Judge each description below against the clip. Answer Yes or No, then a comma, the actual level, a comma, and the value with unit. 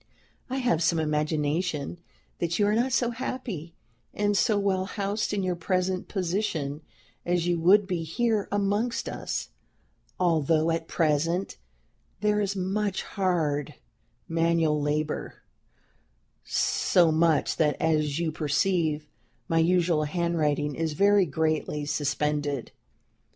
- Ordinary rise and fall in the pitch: Yes, average, 4.3 semitones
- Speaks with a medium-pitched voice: Yes, medium, 170 Hz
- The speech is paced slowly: Yes, slow, 120 wpm